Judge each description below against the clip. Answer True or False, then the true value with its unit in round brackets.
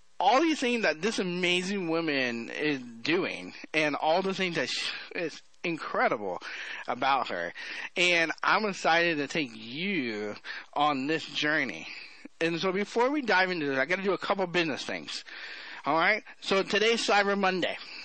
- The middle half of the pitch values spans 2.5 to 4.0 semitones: False (5.1 semitones)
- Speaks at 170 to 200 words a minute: False (160 wpm)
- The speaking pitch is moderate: True (180 Hz)